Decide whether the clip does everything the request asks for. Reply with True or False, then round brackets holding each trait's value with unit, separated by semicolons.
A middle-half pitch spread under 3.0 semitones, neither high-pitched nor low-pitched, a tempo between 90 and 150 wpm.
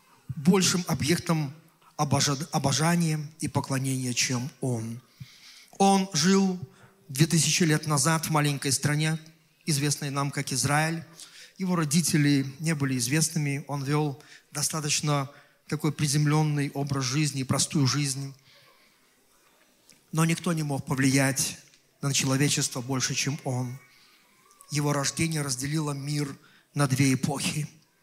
True (2.6 semitones; 150 Hz; 110 wpm)